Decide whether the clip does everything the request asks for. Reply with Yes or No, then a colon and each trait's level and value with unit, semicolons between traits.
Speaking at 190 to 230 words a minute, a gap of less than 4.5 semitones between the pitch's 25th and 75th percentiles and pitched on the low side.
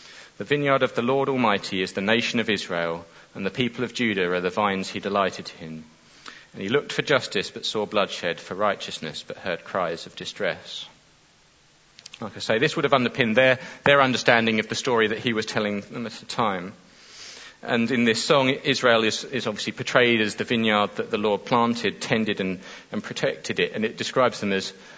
Yes: average, 200 wpm; average, 4.1 semitones; low, 110 Hz